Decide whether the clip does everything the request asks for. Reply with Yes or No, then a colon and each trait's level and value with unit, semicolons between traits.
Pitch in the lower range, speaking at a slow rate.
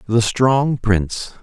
Yes: low, 115 Hz; slow, 125 wpm